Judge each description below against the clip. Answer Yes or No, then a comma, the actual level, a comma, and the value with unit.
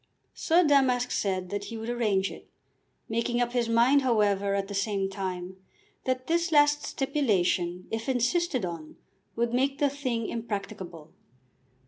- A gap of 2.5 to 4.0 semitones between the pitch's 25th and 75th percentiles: No, average, 5.1 semitones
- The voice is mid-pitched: No, high, 230 Hz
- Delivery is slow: No, average, 145 wpm